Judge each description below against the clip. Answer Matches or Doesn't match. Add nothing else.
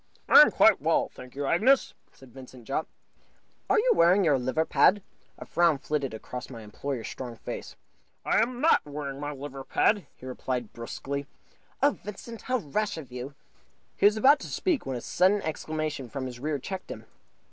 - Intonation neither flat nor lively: Doesn't match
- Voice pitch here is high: Doesn't match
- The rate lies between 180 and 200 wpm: Matches